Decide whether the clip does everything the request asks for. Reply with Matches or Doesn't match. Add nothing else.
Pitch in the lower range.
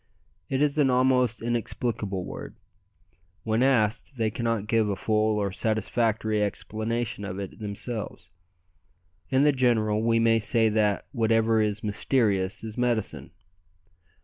Matches